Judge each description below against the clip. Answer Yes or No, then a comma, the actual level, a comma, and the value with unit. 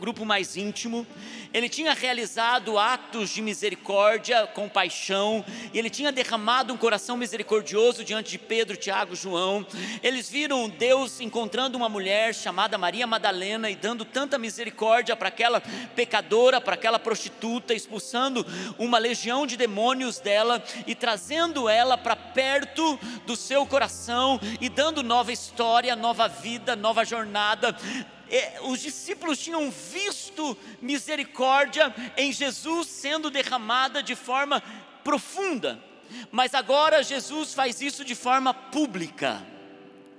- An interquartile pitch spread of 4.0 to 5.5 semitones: No, average, 3.4 semitones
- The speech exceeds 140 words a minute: No, average, 125 wpm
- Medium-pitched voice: No, high, 235 Hz